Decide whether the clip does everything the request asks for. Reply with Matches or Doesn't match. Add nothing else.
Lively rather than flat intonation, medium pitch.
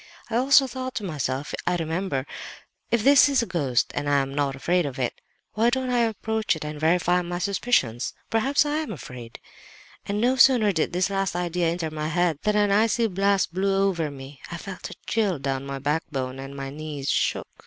Matches